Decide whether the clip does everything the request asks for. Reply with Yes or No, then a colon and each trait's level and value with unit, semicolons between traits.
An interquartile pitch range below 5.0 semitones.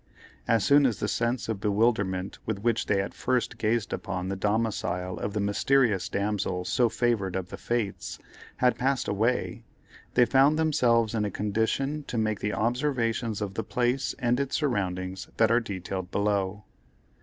Yes: average, 3.7 semitones